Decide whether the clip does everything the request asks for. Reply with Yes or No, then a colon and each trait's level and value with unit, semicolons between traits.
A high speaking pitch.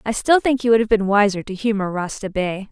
Yes: high, 210 Hz